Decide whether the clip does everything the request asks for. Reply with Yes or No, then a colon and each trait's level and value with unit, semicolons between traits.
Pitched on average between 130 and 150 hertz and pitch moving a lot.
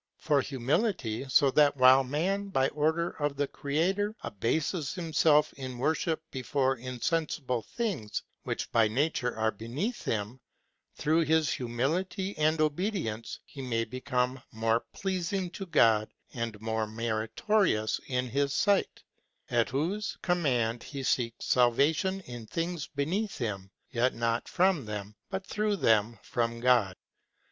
Yes: low, 135 Hz; wide, 6.2 semitones